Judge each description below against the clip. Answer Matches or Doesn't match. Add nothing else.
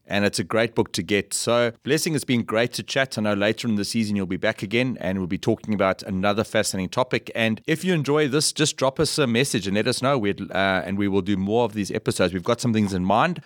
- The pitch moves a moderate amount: Matches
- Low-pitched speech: Matches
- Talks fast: Matches